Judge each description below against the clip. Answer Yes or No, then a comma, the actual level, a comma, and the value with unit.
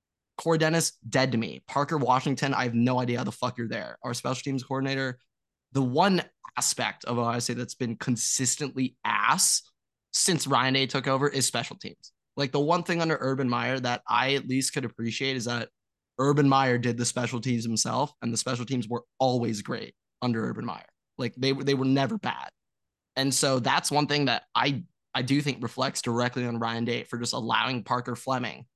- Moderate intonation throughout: No, narrow, 2.2 semitones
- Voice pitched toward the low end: Yes, low, 130 Hz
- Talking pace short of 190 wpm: No, average, 200 wpm